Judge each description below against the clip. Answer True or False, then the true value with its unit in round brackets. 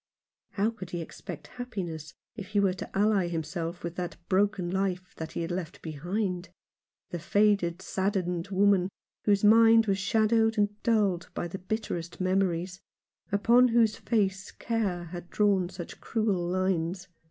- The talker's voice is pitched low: False (190 Hz)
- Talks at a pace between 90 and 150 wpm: True (140 wpm)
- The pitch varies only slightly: False (3.0 semitones)